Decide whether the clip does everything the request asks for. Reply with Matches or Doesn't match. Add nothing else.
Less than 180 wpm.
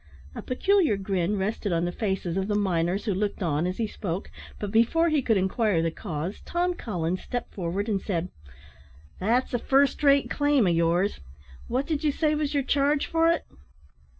Doesn't match